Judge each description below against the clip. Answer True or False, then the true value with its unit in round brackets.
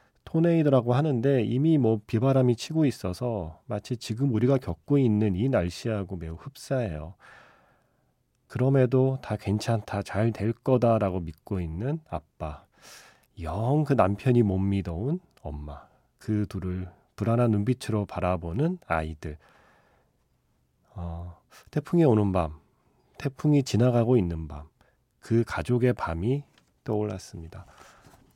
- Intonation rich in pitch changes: True (6.1 semitones)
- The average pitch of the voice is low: True (110 Hz)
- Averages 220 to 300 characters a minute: True (255 characters per minute)